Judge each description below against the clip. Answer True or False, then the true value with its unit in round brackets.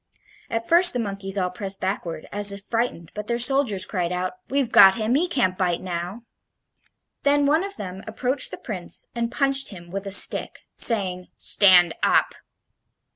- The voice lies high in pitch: True (200 Hz)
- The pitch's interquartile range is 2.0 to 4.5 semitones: False (5.1 semitones)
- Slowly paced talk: False (175 wpm)